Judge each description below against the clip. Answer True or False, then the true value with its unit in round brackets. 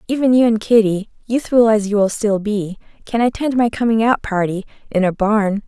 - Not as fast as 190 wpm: False (200 wpm)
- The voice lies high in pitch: True (215 Hz)